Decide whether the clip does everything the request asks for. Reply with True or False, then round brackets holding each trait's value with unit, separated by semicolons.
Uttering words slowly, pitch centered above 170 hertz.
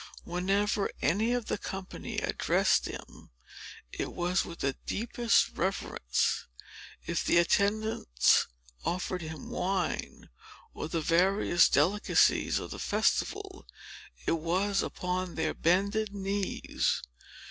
True (110 wpm; 185 Hz)